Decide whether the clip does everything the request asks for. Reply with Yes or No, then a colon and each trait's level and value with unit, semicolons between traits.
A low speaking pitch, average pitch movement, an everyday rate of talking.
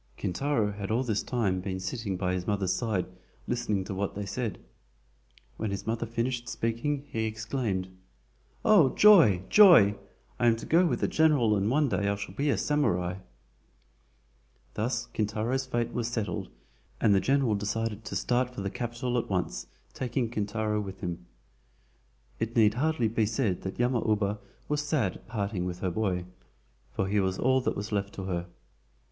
Yes: low, 110 Hz; average, 3.8 semitones; average, 175 wpm